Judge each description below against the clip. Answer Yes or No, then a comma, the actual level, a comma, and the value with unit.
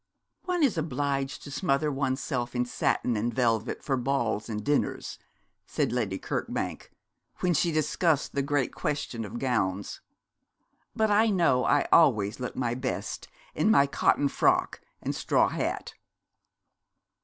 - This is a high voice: No, low, 135 Hz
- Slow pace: No, average, 145 wpm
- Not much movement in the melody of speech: No, average, 3.7 semitones